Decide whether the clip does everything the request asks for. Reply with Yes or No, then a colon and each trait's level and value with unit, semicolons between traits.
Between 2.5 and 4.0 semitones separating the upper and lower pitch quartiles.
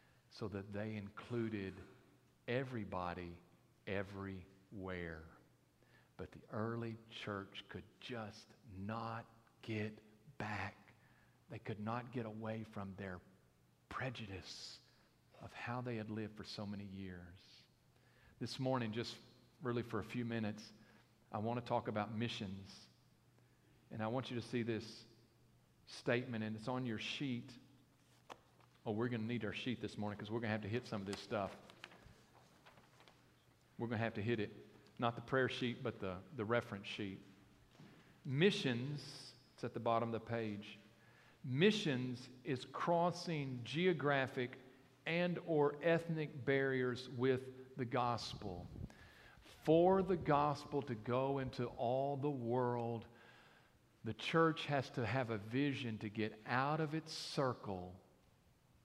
Yes: average, 3.5 semitones